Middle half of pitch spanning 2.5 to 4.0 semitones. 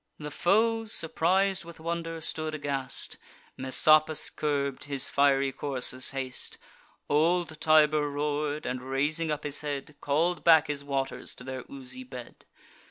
Yes: average, 2.8 semitones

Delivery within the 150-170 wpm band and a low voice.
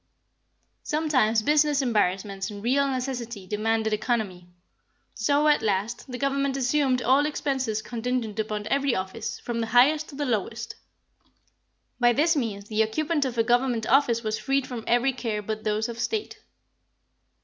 No: average, 155 wpm; high, 240 Hz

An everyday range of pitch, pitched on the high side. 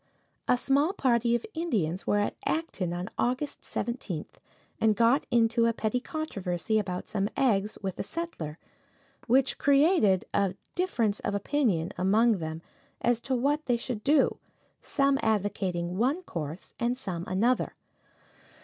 No: wide, 5.9 semitones; high, 225 Hz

